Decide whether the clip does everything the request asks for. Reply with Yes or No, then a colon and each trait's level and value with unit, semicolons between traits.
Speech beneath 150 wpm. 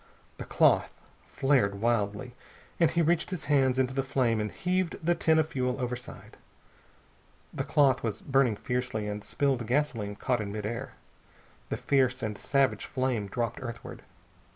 No: average, 155 wpm